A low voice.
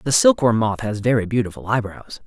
Yes: low, 115 Hz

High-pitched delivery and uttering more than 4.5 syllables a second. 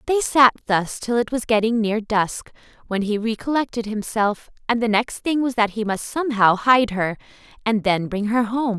Yes: high, 225 Hz; 4.8 syllables/s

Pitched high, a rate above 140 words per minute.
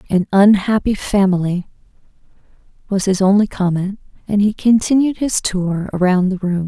No: high, 195 Hz; slow, 135 wpm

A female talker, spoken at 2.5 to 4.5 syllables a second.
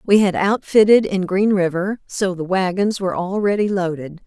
No: female; 4.9 syllables/s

